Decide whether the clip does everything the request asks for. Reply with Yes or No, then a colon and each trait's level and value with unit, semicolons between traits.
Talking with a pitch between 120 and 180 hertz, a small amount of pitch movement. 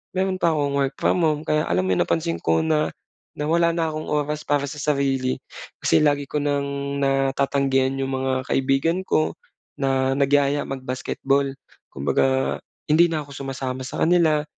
Yes: medium, 140 Hz; narrow, 2.2 semitones